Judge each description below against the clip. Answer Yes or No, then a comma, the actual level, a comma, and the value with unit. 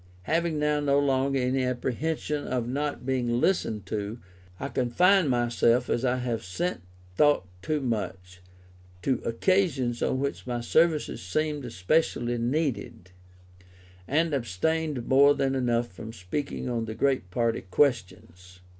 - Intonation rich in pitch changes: No, average, 4.1 semitones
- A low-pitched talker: Yes, low, 125 Hz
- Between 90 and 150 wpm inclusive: Yes, slow, 135 wpm